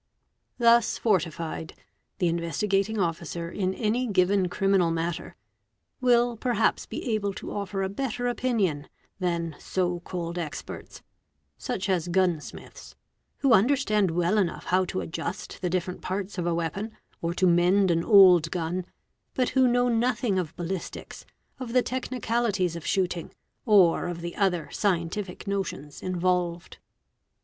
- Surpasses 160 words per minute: No, average, 140 wpm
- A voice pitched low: No, medium, 185 Hz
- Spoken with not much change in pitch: No, average, 3.8 semitones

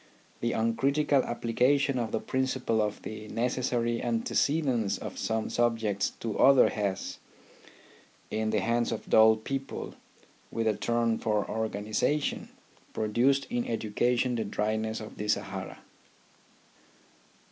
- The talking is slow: Yes, slow, 125 wpm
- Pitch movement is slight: Yes, narrow, 2.3 semitones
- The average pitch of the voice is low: Yes, low, 115 Hz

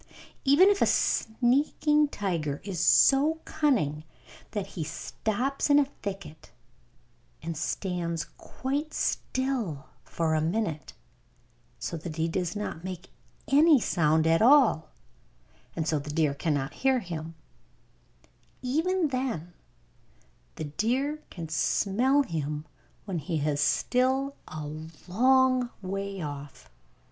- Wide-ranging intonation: Yes, wide, 8.8 semitones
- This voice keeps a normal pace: No, slow, 115 wpm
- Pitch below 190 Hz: No, high, 195 Hz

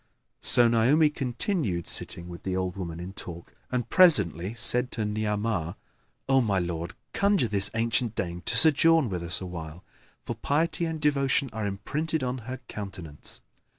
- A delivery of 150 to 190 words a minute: Yes, average, 160 wpm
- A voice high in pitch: No, low, 110 Hz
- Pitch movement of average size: No, wide, 7.0 semitones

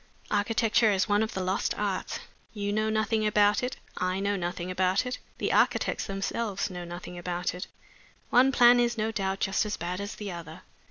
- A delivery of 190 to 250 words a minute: Yes, average, 195 wpm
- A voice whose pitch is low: No, high, 200 Hz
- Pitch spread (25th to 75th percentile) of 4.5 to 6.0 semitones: No, average, 3.0 semitones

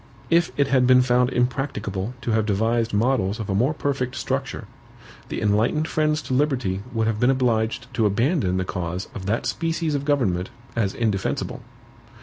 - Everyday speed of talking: Yes, average, 170 wpm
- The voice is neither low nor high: No, low, 120 Hz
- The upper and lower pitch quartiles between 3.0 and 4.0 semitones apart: No, average, 4.6 semitones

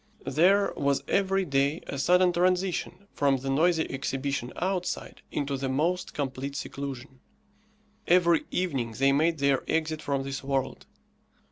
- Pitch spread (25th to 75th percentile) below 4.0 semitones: No, average, 4.6 semitones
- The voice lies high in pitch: No, medium, 140 Hz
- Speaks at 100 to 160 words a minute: Yes, slow, 135 wpm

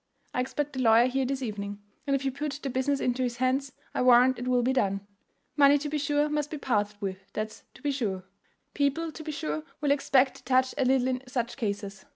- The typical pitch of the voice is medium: No, very high, 260 Hz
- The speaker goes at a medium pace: No, fast, 230 wpm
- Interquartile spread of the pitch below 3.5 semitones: Yes, average, 3.0 semitones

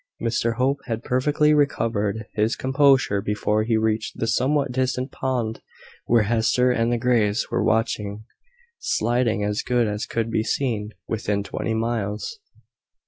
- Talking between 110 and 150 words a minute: Yes, average, 140 wpm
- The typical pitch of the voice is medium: No, low, 115 Hz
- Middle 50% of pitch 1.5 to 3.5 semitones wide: Yes, average, 2.8 semitones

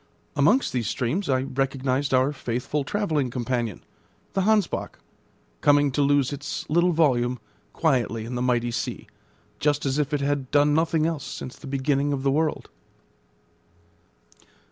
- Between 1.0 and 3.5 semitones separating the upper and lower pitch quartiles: Yes, average, 2.7 semitones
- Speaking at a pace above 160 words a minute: No, average, 145 wpm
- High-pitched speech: No, medium, 140 Hz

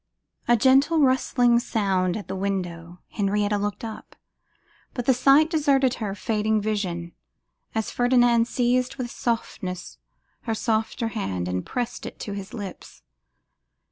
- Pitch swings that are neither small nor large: Yes, average, 3.9 semitones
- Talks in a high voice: Yes, high, 220 Hz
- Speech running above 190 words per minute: No, slow, 135 wpm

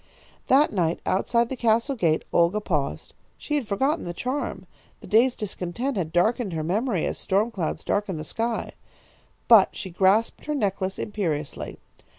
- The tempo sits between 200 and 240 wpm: No, average, 160 wpm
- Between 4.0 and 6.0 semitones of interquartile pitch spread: Yes, average, 5.2 semitones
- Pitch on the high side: Yes, high, 205 Hz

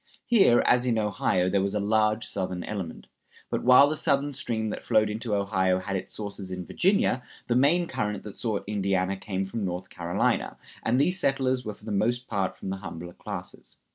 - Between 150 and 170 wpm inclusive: No, average, 200 wpm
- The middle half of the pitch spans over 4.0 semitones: Yes, average, 4.6 semitones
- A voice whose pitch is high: No, low, 105 Hz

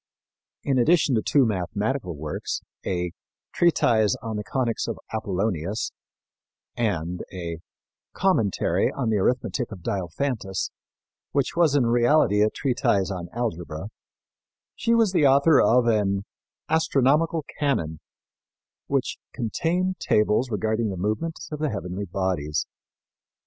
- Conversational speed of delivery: No, slow, 120 wpm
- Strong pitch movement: Yes, wide, 6.4 semitones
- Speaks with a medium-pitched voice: No, low, 110 Hz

